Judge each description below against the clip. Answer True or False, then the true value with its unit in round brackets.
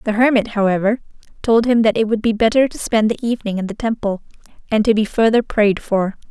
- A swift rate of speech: True (220 wpm)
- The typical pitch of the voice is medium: False (220 Hz)